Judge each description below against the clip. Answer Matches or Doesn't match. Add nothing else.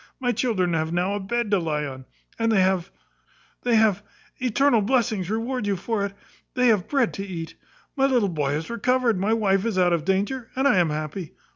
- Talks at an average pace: Doesn't match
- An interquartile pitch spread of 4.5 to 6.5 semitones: Matches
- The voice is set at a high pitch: Matches